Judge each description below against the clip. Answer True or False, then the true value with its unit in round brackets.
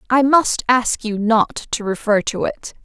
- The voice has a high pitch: True (230 Hz)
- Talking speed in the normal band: True (190 wpm)